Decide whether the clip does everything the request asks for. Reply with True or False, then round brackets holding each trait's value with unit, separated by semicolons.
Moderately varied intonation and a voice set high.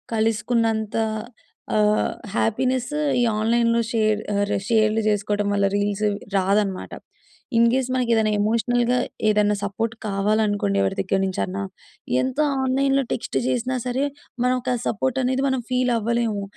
True (3.2 semitones; 225 Hz)